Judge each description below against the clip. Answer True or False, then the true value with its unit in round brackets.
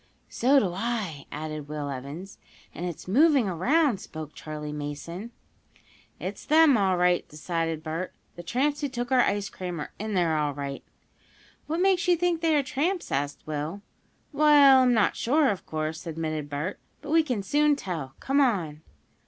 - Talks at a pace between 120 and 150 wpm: False (170 wpm)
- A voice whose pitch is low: False (190 Hz)